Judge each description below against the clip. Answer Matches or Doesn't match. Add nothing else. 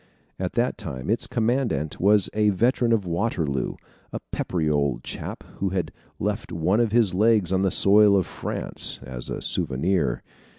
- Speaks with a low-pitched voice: Matches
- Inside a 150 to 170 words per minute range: Matches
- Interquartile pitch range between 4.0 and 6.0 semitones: Matches